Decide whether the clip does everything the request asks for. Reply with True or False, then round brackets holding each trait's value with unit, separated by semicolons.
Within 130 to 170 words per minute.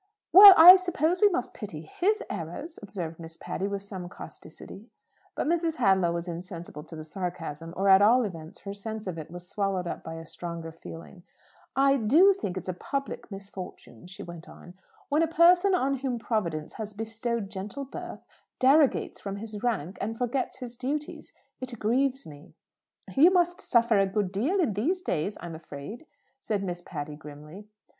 False (180 wpm)